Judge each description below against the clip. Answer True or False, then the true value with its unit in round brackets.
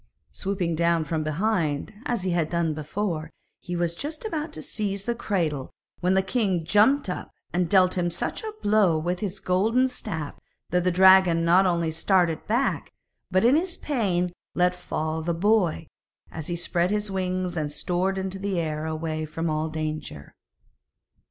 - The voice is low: False (180 Hz)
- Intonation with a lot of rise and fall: False (3.7 semitones)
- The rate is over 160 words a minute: True (170 wpm)